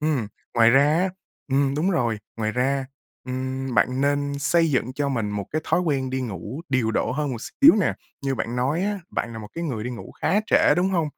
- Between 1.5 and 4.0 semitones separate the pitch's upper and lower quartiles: Yes, average, 3.7 semitones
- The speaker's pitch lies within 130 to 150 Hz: Yes, low, 135 Hz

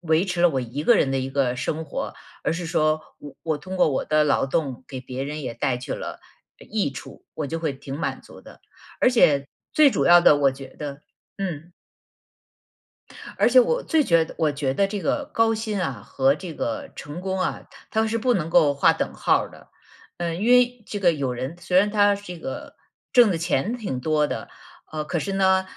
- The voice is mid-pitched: Yes, medium, 160 Hz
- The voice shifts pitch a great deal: Yes, wide, 5.9 semitones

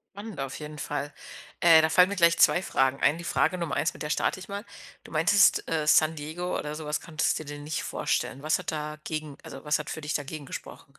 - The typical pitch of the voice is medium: Yes, medium, 155 Hz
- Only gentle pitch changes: Yes, narrow, 2.3 semitones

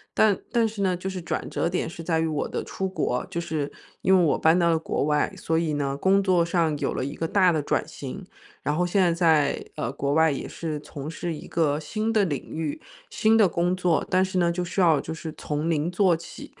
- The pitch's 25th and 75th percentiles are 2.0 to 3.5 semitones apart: Yes, average, 3.1 semitones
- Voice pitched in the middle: Yes, medium, 170 Hz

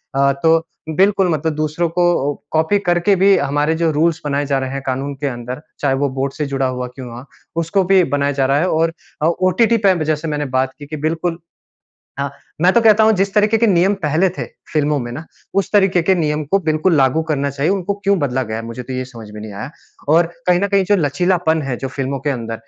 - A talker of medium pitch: Yes, medium, 155 Hz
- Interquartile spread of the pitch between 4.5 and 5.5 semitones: Yes, average, 4.8 semitones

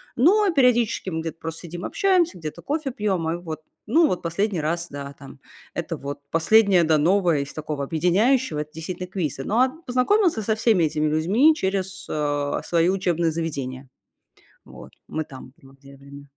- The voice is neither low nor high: Yes, medium, 170 Hz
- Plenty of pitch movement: Yes, wide, 6.0 semitones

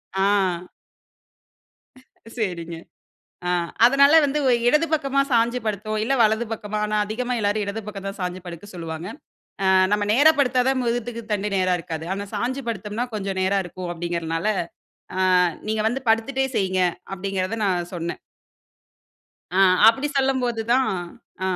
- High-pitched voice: Yes, high, 210 Hz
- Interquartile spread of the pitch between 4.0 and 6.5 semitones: Yes, average, 4.6 semitones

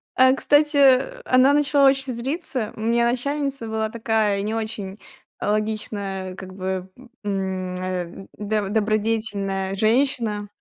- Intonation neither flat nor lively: Yes, average, 4.6 semitones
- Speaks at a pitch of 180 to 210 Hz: No, high, 220 Hz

